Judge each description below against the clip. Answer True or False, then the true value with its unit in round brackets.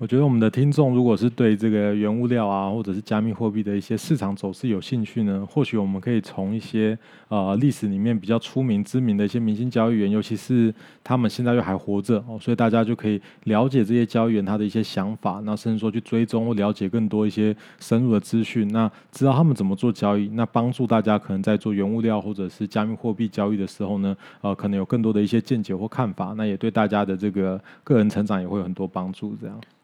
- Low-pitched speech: True (110 Hz)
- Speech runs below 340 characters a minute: False (370 characters per minute)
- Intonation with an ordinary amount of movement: False (2.1 semitones)